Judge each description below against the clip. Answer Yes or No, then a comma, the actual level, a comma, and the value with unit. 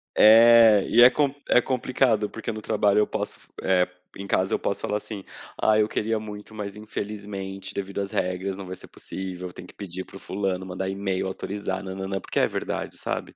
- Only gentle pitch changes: Yes, narrow, 2.2 semitones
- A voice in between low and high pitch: No, low, 100 Hz